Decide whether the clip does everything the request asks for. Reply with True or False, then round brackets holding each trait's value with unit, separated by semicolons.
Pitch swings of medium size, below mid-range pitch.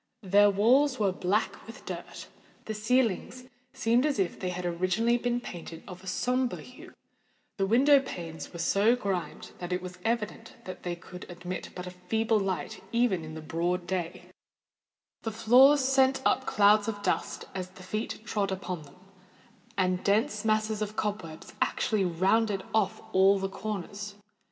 False (3.7 semitones; 200 Hz)